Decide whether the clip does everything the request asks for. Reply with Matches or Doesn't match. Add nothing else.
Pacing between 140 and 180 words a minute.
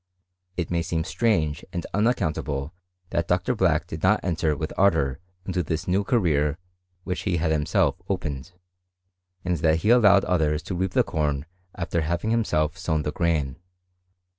Matches